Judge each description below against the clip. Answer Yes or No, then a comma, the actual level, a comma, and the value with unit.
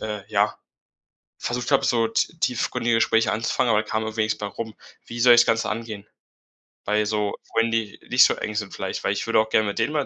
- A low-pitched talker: Yes, low, 110 Hz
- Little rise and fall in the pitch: Yes, narrow, 1.7 semitones